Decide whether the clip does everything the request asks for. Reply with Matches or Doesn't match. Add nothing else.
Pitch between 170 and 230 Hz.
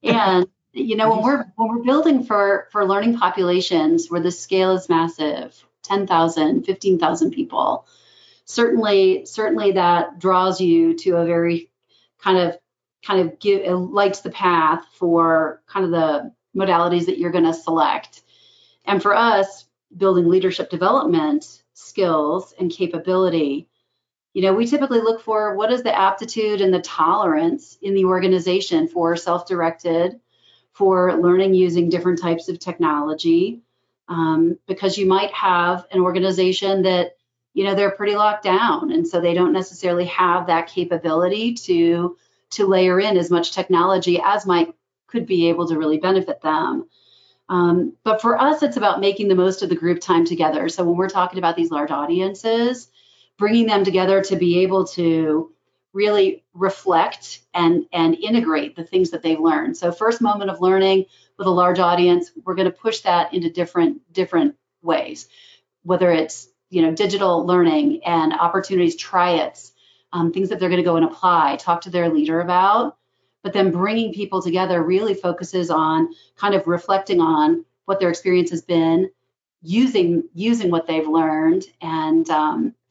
Matches